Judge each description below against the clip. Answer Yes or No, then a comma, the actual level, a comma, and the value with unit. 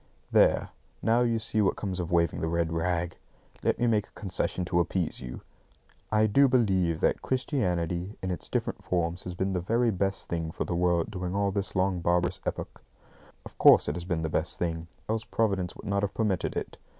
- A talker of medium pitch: No, very low, 90 Hz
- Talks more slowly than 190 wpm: No, fast, 205 wpm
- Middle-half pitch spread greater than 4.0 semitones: No, average, 3.3 semitones